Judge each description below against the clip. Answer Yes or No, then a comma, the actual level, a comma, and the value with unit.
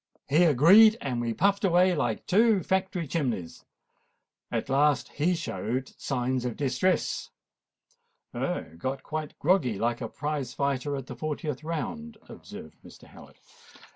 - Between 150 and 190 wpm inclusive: No, average, 140 wpm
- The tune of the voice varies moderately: No, wide, 5.8 semitones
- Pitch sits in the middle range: Yes, medium, 145 Hz